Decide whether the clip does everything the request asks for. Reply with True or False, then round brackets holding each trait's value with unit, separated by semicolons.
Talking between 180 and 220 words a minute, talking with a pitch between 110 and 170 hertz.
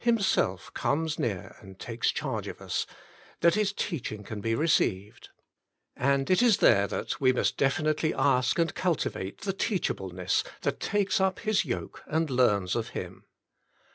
False (155 wpm; 140 Hz)